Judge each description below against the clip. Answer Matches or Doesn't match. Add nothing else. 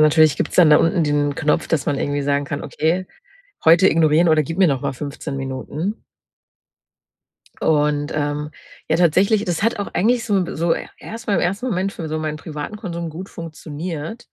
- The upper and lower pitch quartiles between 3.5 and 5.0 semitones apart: Matches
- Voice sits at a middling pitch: Matches